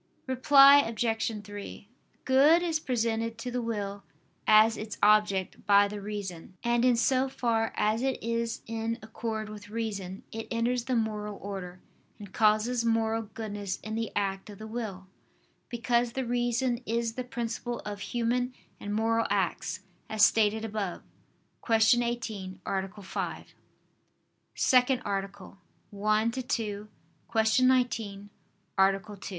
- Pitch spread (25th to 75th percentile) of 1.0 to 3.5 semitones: Yes, narrow, 2.6 semitones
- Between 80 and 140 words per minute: Yes, slow, 135 wpm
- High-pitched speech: Yes, high, 225 Hz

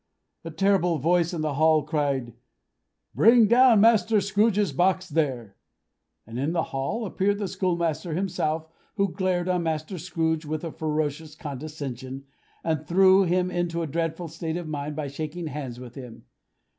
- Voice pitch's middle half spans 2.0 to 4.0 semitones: Yes, average, 3.6 semitones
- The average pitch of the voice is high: No, medium, 165 Hz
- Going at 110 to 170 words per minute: Yes, average, 155 wpm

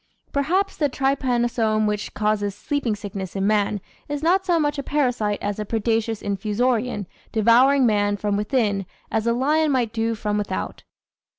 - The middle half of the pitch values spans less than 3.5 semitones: No, average, 4.5 semitones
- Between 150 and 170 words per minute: Yes, average, 160 wpm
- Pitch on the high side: Yes, high, 225 Hz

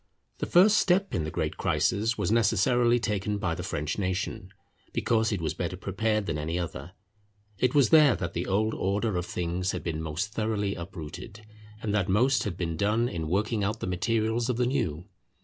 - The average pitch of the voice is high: No, low, 100 Hz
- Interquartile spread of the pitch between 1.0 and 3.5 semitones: No, average, 4.4 semitones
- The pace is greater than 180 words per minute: Yes, average, 195 wpm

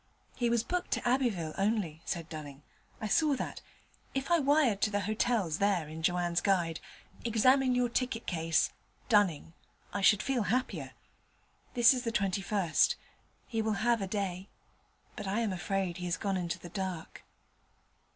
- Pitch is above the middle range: Yes, high, 200 Hz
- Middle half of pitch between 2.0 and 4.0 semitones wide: No, average, 5.2 semitones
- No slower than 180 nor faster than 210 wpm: No, average, 160 wpm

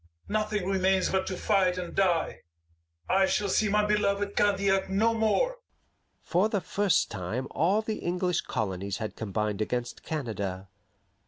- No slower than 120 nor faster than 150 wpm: Yes, average, 145 wpm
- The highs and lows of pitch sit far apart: Yes, wide, 8.7 semitones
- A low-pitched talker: No, high, 190 Hz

